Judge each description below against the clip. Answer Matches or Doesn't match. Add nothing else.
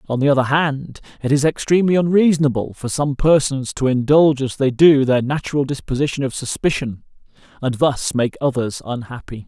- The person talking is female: Doesn't match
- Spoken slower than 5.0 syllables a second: Doesn't match